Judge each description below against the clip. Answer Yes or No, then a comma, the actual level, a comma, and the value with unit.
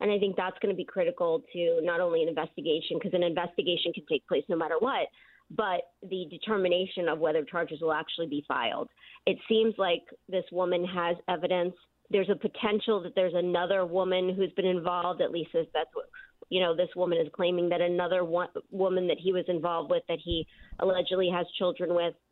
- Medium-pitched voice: Yes, medium, 180 Hz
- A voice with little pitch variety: Yes, narrow, 2.2 semitones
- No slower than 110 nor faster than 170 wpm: No, average, 200 wpm